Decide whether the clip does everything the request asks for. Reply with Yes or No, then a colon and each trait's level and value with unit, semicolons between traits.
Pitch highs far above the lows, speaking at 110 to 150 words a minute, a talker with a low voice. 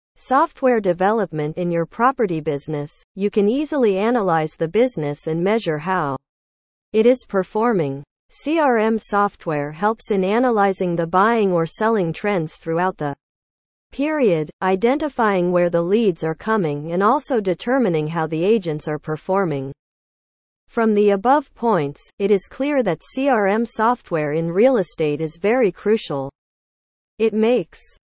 No: wide, 6.2 semitones; slow, 135 wpm; high, 190 Hz